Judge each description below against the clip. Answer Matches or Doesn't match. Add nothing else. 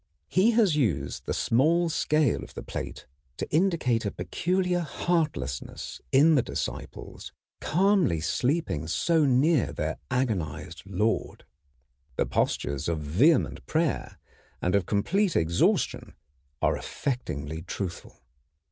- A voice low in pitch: Matches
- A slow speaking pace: Matches